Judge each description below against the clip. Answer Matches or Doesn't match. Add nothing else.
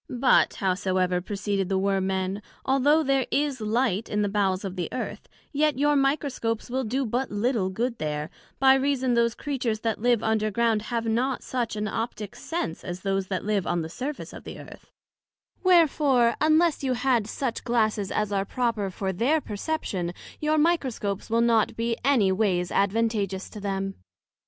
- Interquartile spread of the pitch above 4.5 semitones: Matches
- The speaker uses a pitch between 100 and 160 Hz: Doesn't match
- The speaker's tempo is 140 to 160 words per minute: Doesn't match